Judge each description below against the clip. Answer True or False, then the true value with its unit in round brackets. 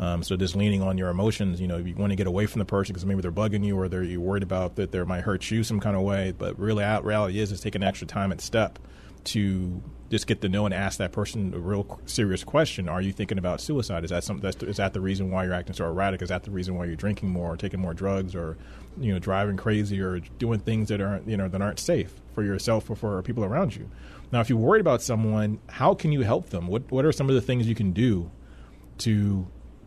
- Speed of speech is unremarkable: False (270 wpm)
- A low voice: True (100 Hz)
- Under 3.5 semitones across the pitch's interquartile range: True (2.4 semitones)